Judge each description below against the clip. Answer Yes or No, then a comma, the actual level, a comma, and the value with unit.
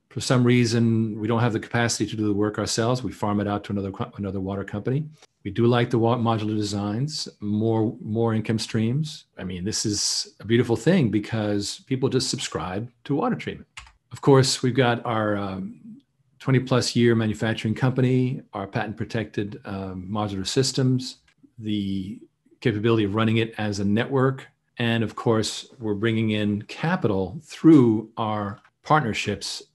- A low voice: Yes, low, 115 Hz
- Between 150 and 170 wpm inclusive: Yes, average, 160 wpm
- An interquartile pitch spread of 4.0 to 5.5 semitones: No, average, 3.3 semitones